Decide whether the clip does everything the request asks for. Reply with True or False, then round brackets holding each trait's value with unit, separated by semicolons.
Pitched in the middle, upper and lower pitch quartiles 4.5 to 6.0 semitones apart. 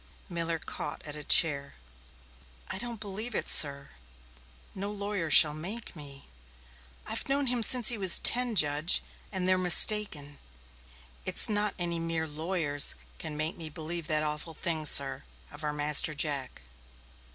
True (165 Hz; 5.0 semitones)